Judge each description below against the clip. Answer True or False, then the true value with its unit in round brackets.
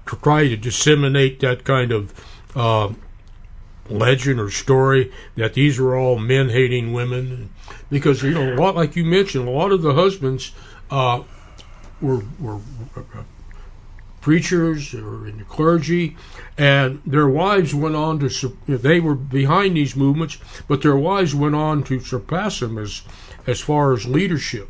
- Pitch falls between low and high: False (130 Hz)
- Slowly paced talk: False (160 wpm)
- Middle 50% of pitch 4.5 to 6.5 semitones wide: True (5.0 semitones)